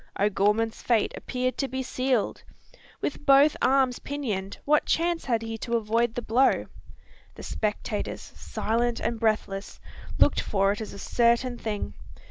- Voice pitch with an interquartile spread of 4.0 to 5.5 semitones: No, average, 3.4 semitones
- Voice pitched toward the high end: Yes, high, 235 Hz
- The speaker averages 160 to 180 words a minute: No, average, 145 wpm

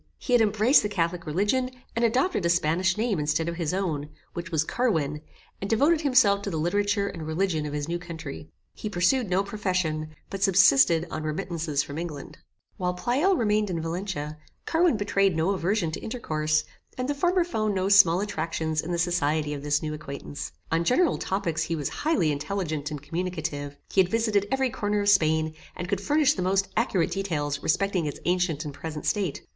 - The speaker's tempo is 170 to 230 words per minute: Yes, average, 190 wpm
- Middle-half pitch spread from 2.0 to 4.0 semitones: No, average, 4.7 semitones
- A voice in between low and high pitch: Yes, medium, 180 Hz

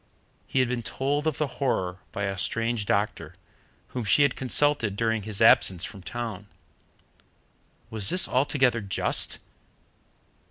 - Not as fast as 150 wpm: Yes, slow, 135 wpm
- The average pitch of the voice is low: Yes, low, 115 Hz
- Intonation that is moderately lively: Yes, average, 4.7 semitones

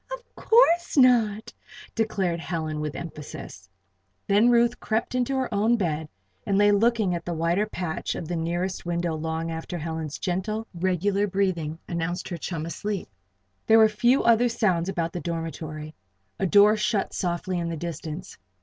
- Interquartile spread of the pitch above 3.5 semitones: Yes, average, 4.4 semitones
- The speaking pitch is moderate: Yes, medium, 180 Hz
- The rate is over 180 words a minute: No, average, 165 wpm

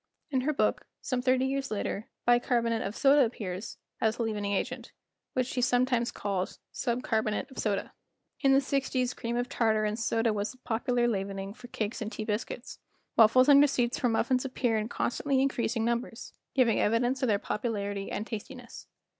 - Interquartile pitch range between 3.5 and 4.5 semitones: No, average, 2.9 semitones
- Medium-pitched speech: No, high, 235 Hz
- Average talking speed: Yes, average, 180 wpm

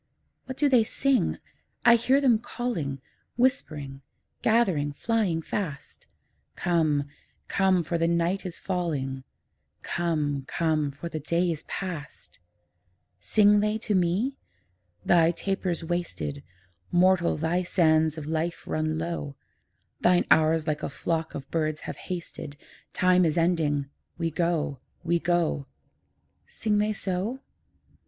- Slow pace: Yes, slow, 125 wpm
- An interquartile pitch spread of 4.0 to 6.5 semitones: No, average, 3.6 semitones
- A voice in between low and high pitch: Yes, medium, 170 Hz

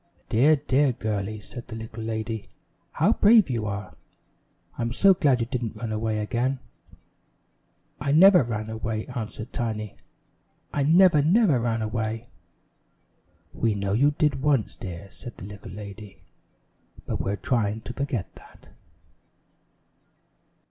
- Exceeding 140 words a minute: No, slow, 135 wpm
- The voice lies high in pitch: No, low, 115 Hz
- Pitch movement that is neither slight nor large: Yes, average, 4.3 semitones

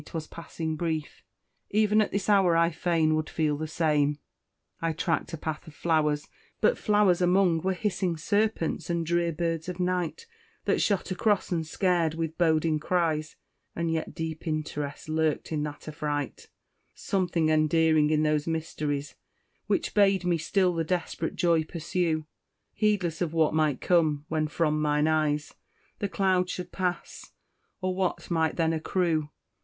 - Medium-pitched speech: Yes, medium, 165 Hz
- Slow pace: No, average, 155 wpm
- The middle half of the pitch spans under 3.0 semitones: Yes, narrow, 2.5 semitones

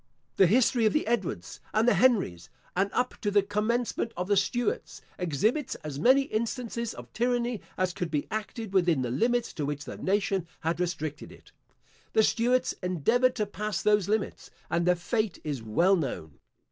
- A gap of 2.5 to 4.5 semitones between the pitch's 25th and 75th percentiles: No, wide, 5.5 semitones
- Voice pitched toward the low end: No, high, 205 Hz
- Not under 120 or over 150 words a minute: No, average, 175 wpm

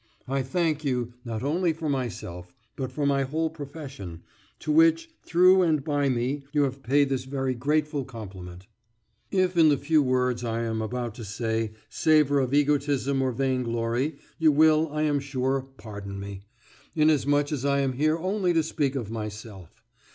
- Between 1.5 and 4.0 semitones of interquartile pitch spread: No, average, 4.4 semitones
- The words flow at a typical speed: Yes, average, 165 wpm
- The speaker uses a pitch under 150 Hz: Yes, low, 135 Hz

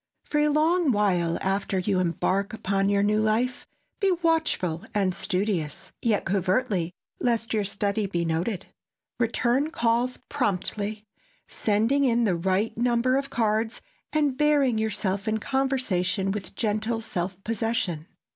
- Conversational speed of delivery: No, slow, 130 wpm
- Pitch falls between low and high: No, high, 215 Hz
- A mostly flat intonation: No, average, 4.2 semitones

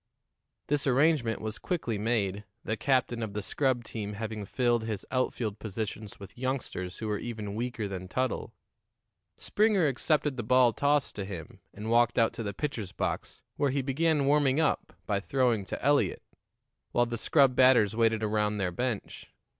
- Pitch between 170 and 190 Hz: No, low, 115 Hz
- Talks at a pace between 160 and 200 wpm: Yes, average, 170 wpm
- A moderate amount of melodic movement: Yes, average, 4.0 semitones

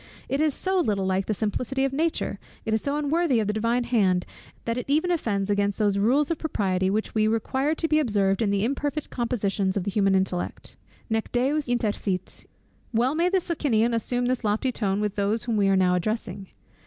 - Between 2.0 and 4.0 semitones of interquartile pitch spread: No, wide, 5.4 semitones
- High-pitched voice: Yes, high, 225 Hz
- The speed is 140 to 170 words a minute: No, average, 195 wpm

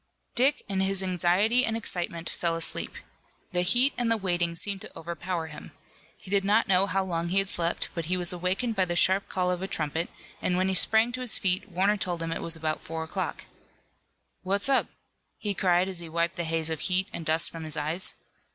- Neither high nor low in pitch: Yes, medium, 180 Hz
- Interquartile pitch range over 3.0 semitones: No, average, 2.7 semitones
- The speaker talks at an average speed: No, fast, 220 wpm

